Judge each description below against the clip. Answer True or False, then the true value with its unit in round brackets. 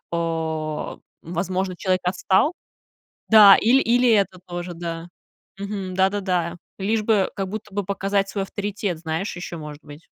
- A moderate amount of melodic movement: True (3.0 semitones)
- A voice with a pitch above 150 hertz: True (190 Hz)